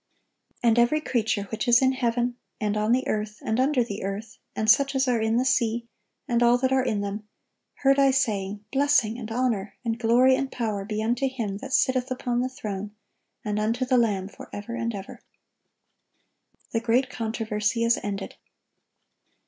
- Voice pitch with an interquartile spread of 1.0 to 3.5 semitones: Yes, average, 3.2 semitones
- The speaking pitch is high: Yes, high, 230 Hz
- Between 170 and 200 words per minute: Yes, average, 180 wpm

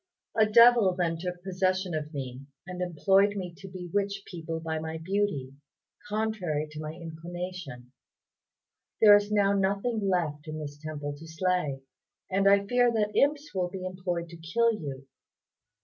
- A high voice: No, medium, 180 Hz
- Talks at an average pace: Yes, average, 155 wpm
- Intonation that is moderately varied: Yes, average, 4.0 semitones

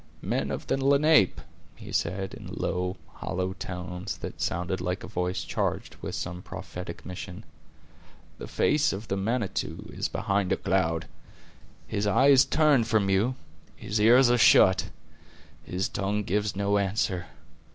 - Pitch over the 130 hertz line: No, low, 100 Hz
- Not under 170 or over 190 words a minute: No, average, 150 wpm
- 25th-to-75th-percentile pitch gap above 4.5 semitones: No, average, 3.6 semitones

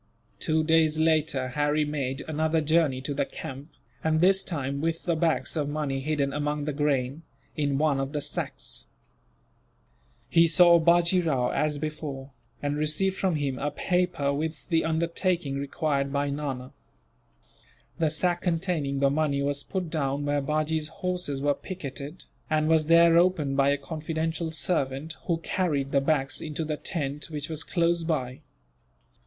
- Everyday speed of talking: Yes, average, 160 wpm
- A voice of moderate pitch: Yes, medium, 150 Hz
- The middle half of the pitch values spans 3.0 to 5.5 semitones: No, narrow, 2.6 semitones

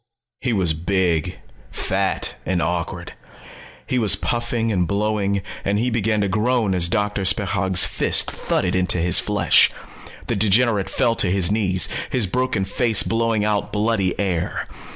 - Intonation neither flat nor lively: Yes, average, 3.4 semitones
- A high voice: No, low, 100 Hz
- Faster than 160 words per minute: No, average, 150 wpm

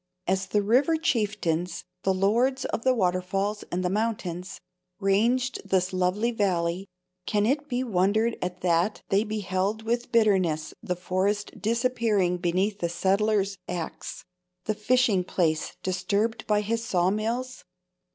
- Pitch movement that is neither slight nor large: Yes, average, 3.7 semitones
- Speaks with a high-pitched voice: Yes, high, 200 Hz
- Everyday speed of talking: No, slow, 130 wpm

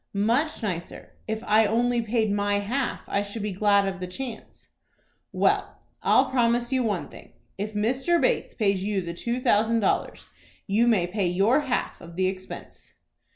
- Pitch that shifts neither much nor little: Yes, average, 3.4 semitones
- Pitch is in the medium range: No, high, 215 Hz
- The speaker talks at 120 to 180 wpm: Yes, average, 170 wpm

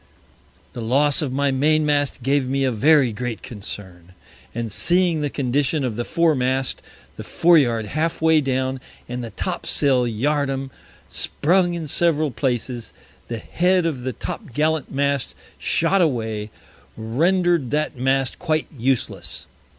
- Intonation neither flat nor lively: Yes, average, 4.1 semitones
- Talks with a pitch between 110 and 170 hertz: Yes, low, 135 Hz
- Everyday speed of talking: Yes, average, 150 wpm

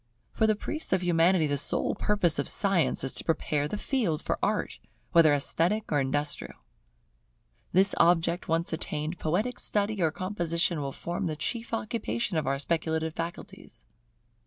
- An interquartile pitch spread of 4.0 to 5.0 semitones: Yes, average, 4.3 semitones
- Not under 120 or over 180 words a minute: Yes, average, 160 wpm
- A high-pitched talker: No, medium, 170 Hz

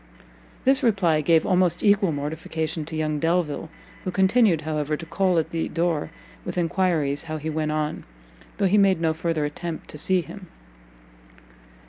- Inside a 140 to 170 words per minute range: Yes, average, 160 wpm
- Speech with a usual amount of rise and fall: Yes, average, 3.0 semitones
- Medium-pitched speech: Yes, medium, 165 Hz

